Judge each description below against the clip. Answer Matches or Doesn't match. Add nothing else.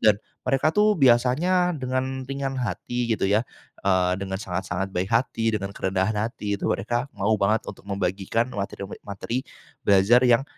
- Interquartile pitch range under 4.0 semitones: Doesn't match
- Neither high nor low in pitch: Doesn't match